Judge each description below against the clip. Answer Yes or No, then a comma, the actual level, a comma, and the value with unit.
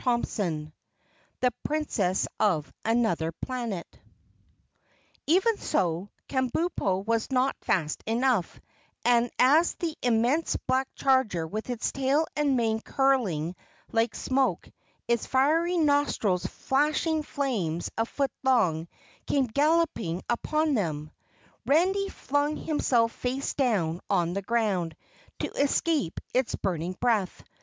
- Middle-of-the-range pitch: No, high, 240 Hz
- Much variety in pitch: Yes, wide, 6.8 semitones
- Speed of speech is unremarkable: No, slow, 115 wpm